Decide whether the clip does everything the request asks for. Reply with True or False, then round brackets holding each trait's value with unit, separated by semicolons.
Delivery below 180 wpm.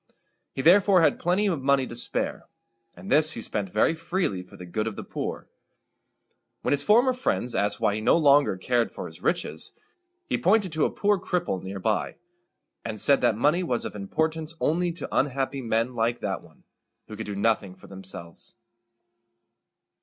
False (185 wpm)